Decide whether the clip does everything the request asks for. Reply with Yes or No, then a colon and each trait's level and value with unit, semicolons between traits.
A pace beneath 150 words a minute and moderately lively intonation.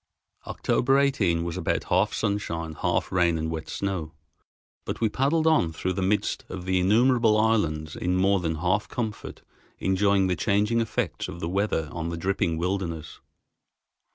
No: average, 160 wpm; average, 4.2 semitones